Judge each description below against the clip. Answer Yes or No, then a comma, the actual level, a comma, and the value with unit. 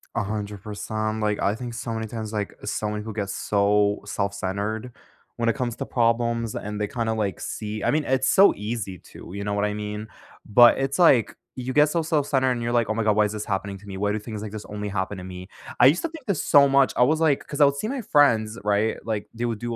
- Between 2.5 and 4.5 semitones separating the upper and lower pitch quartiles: Yes, average, 3.2 semitones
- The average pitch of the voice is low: Yes, low, 110 Hz